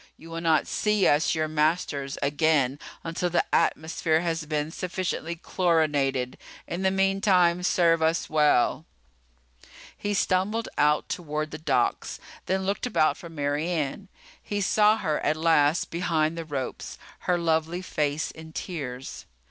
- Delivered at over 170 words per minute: No, average, 140 wpm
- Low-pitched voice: No, medium, 160 Hz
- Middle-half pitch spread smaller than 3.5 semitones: Yes, average, 3.1 semitones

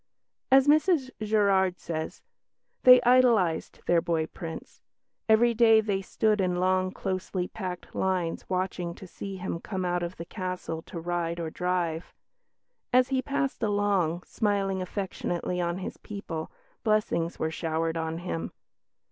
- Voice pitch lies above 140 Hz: Yes, medium, 185 Hz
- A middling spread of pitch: Yes, average, 3.8 semitones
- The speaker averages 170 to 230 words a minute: No, average, 140 wpm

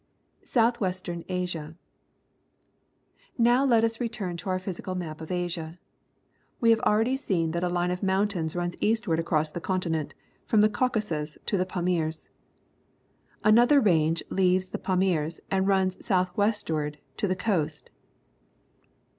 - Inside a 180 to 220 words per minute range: No, average, 155 wpm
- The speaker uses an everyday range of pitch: Yes, average, 4.0 semitones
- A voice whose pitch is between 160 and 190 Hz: Yes, medium, 185 Hz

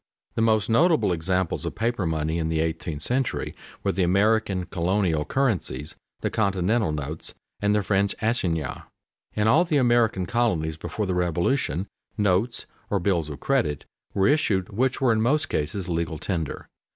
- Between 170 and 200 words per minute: No, average, 160 wpm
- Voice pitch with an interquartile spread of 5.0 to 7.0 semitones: Yes, wide, 5.4 semitones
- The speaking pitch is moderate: No, very low, 95 Hz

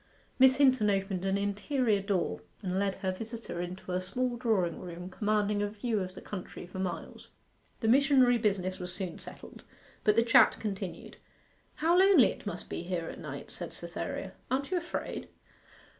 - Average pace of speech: Yes, average, 175 wpm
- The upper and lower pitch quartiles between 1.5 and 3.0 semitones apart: No, average, 4.7 semitones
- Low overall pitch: No, high, 205 Hz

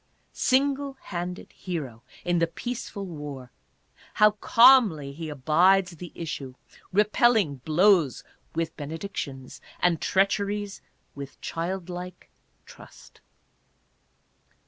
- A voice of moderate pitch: Yes, medium, 175 Hz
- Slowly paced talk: Yes, slow, 95 wpm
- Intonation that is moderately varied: Yes, average, 4.9 semitones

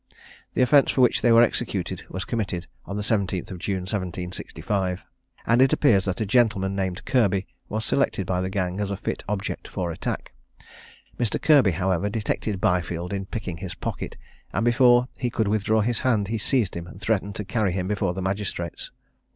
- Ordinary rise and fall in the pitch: Yes, average, 3.3 semitones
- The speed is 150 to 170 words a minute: No, average, 185 wpm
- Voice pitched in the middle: No, low, 100 Hz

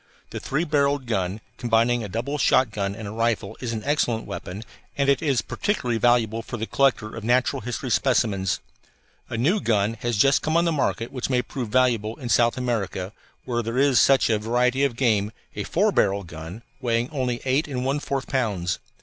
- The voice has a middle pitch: No, low, 120 Hz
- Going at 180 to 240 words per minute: Yes, average, 195 wpm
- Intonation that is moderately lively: Yes, average, 3.6 semitones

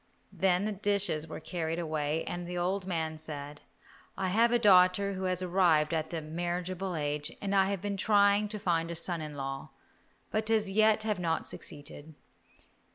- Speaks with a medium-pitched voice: Yes, medium, 180 Hz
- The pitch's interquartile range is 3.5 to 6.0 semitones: Yes, average, 3.9 semitones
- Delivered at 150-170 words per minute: No, average, 180 wpm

